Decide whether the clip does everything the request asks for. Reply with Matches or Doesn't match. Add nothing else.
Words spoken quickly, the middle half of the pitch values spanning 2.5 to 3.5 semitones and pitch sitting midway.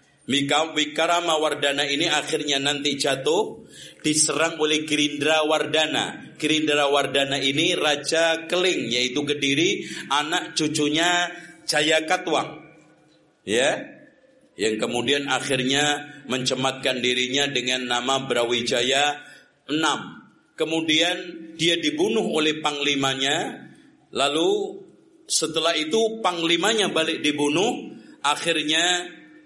Doesn't match